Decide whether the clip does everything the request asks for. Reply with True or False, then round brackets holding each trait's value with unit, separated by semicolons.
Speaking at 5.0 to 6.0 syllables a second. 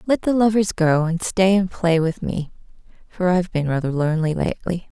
True (5.5 syllables/s)